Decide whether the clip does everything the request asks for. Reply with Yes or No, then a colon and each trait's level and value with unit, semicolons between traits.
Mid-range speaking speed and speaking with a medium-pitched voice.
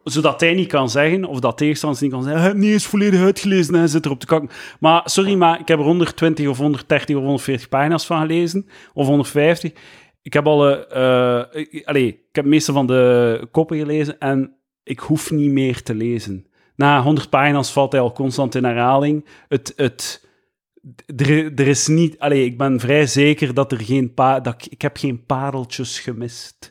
Yes: average, 175 wpm; medium, 145 Hz